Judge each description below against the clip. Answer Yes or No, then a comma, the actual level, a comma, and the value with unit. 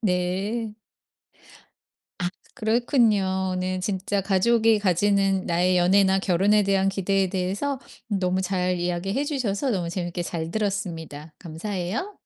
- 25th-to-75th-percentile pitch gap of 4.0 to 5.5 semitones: No, narrow, 2.4 semitones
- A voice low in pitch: No, high, 190 Hz